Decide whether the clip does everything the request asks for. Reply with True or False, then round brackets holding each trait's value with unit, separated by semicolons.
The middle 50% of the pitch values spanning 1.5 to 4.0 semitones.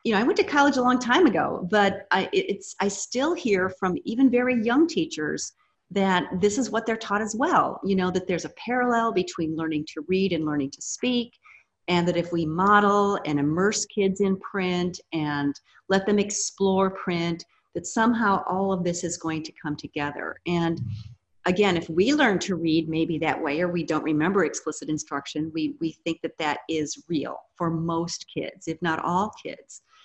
False (4.5 semitones)